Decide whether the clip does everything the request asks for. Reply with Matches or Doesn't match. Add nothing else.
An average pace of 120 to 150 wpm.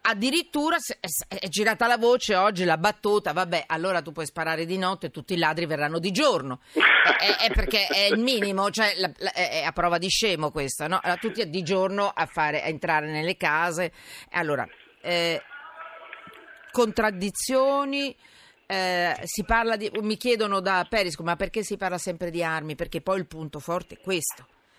Doesn't match